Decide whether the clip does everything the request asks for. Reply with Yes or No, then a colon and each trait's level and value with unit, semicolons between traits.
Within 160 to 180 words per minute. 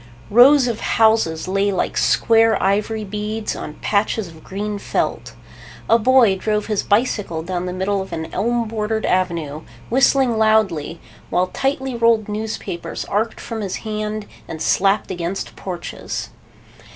No: average, 140 wpm